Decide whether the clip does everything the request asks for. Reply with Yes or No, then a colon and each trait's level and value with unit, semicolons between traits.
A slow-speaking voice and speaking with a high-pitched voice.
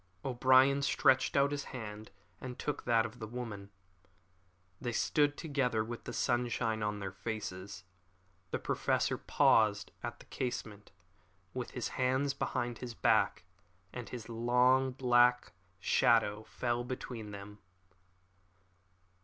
No: slow, 125 wpm; low, 120 Hz